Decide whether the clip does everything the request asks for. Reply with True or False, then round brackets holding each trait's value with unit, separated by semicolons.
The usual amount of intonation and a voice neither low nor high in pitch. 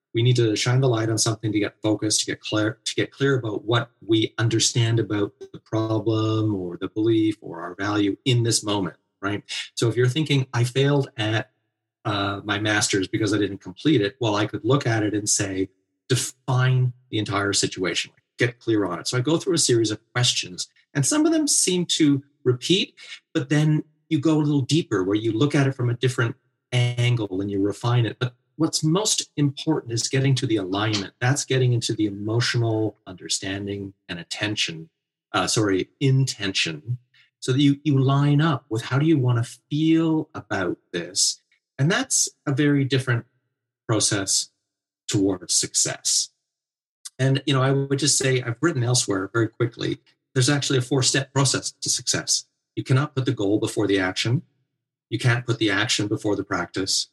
False (4.5 semitones; 120 Hz)